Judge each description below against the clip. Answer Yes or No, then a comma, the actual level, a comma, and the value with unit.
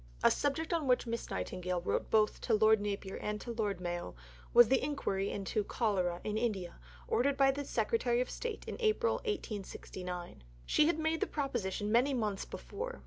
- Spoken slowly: No, average, 180 wpm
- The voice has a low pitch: No, high, 220 Hz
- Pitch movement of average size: No, wide, 6.0 semitones